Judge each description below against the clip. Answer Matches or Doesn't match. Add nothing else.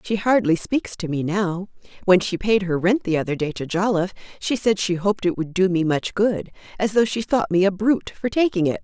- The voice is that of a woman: Matches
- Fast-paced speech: Matches